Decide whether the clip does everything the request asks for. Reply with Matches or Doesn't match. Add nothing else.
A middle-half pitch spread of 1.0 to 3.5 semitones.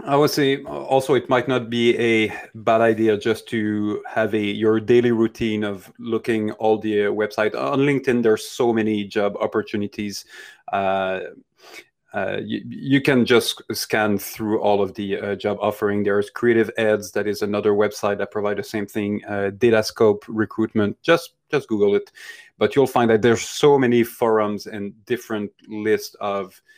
Matches